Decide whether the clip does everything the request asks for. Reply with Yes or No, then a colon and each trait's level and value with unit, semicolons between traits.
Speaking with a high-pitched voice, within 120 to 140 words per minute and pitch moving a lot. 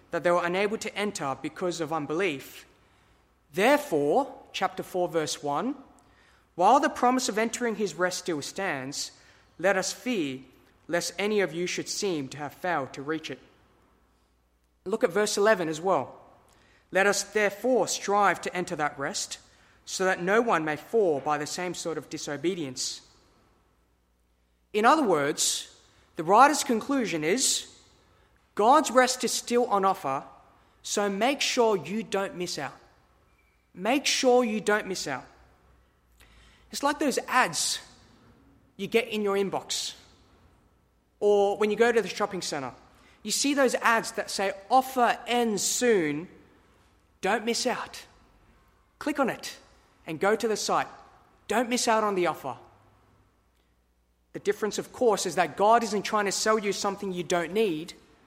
No: high, 195 Hz; average, 155 wpm; wide, 6.9 semitones